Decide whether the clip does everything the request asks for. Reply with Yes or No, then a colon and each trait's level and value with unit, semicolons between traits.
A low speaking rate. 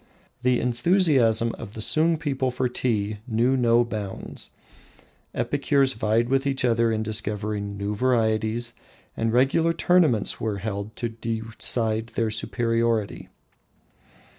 Yes: slow, 120 wpm